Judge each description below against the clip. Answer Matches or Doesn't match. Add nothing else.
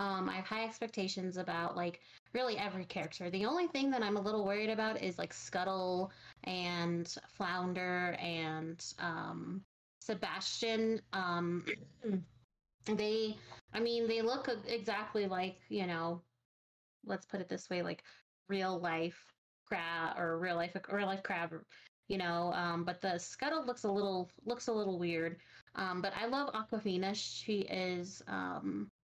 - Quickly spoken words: Doesn't match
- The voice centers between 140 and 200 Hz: Matches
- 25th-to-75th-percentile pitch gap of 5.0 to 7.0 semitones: Doesn't match